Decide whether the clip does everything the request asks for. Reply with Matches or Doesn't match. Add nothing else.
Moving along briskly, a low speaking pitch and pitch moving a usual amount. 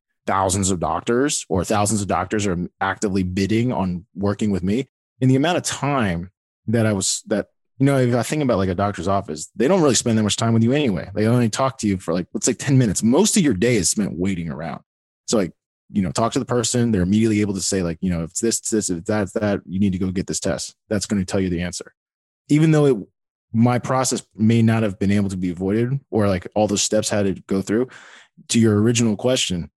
Matches